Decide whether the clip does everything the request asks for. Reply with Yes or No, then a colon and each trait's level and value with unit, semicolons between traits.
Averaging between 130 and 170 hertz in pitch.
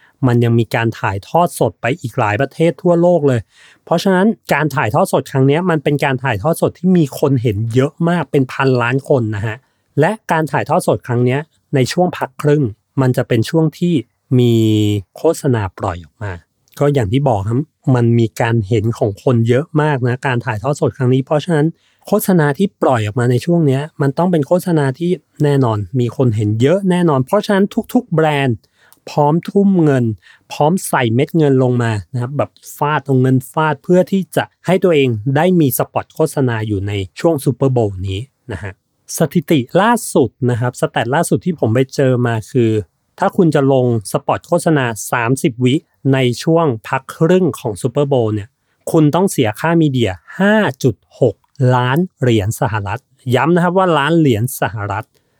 Yes: low, 135 Hz